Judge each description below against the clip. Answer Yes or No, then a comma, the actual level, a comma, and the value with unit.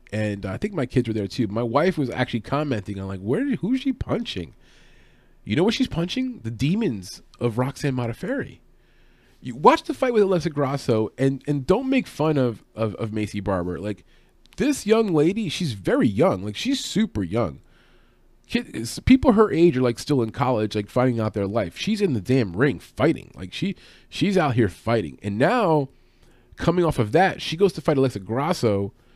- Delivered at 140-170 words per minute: No, average, 195 wpm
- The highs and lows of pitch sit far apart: Yes, wide, 8.6 semitones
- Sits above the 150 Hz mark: No, low, 135 Hz